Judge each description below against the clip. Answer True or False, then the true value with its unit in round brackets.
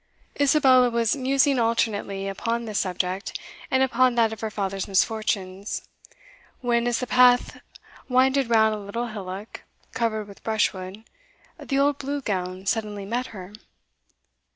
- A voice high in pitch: True (225 Hz)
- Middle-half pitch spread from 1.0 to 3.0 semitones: False (4.0 semitones)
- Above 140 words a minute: False (135 wpm)